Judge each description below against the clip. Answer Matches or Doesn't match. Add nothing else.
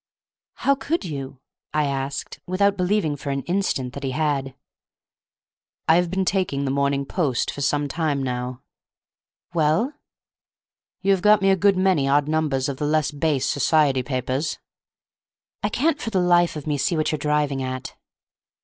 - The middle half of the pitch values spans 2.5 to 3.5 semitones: Doesn't match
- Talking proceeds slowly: Doesn't match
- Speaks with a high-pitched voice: Doesn't match